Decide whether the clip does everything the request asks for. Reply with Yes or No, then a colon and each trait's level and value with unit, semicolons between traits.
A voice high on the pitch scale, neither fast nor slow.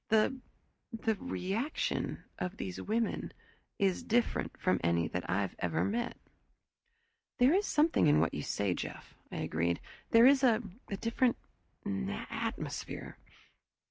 No: high, 220 Hz; slow, 125 wpm